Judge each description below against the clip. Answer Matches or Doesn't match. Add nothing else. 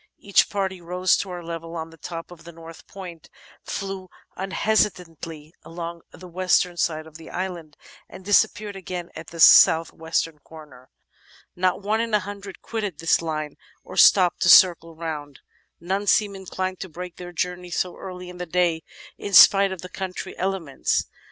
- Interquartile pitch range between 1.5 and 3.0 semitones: Matches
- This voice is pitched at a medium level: Matches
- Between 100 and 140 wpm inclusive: Doesn't match